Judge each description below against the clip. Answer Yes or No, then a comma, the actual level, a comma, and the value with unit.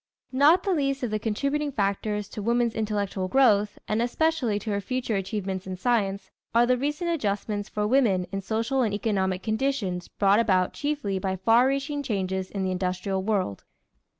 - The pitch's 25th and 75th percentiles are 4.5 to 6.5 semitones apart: Yes, average, 4.8 semitones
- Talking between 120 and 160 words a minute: No, average, 175 wpm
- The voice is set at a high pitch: Yes, high, 215 Hz